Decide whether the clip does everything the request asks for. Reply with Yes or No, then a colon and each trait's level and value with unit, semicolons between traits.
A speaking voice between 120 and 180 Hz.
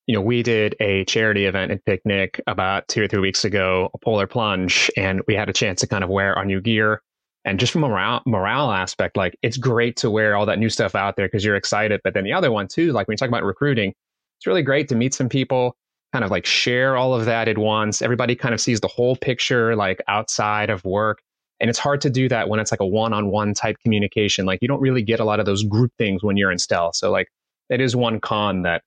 No: low, 110 Hz